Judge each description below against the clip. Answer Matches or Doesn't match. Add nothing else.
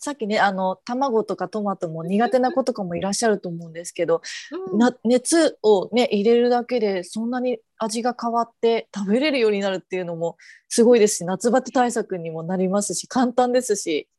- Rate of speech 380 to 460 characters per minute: Matches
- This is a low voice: Doesn't match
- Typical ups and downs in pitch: Matches